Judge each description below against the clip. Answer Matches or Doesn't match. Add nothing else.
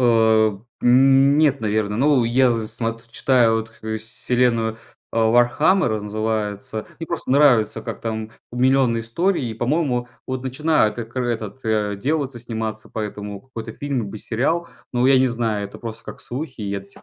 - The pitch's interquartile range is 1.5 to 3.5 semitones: Matches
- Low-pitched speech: Matches